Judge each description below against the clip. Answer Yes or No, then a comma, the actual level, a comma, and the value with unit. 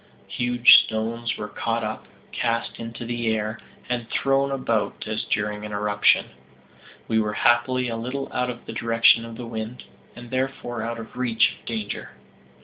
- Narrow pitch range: Yes, narrow, 1.8 semitones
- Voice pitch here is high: No, low, 115 Hz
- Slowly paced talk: No, average, 165 wpm